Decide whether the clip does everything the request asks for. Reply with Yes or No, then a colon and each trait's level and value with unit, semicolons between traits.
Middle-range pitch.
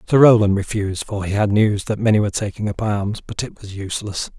No: low, 105 Hz